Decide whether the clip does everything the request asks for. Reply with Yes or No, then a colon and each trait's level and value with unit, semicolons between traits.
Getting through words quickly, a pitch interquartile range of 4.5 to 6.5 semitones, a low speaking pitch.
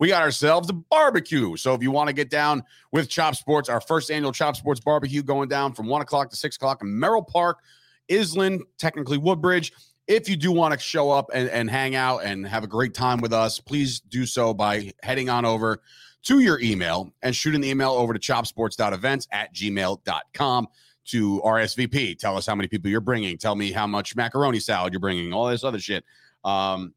Yes: fast, 210 wpm; average, 5.1 semitones; low, 130 Hz